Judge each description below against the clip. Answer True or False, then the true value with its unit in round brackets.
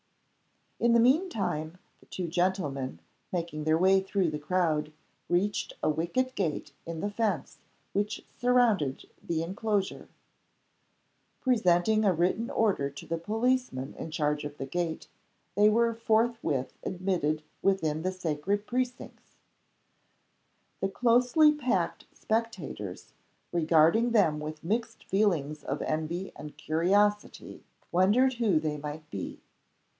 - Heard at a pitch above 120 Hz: True (185 Hz)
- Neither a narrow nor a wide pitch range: False (6.1 semitones)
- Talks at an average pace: False (125 wpm)